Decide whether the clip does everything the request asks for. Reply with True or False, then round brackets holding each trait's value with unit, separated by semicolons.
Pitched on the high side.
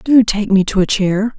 True (205 Hz)